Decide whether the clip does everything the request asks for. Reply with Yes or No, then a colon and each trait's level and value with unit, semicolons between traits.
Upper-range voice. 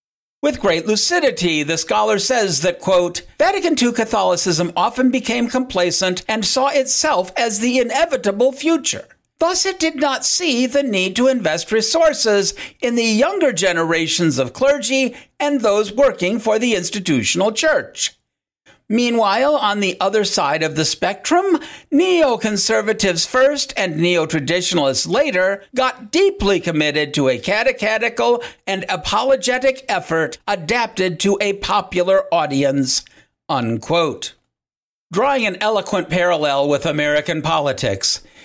Yes: high, 215 Hz